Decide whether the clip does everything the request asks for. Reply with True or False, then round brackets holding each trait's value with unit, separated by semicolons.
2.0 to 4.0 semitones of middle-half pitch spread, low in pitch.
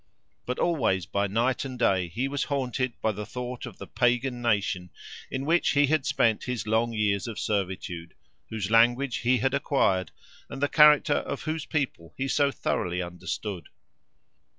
False (5.2 semitones; 120 Hz)